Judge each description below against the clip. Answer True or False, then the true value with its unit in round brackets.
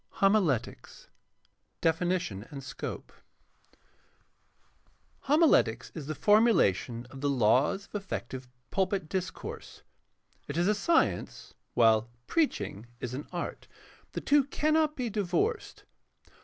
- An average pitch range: False (8.9 semitones)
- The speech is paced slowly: True (110 wpm)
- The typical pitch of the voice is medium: True (175 Hz)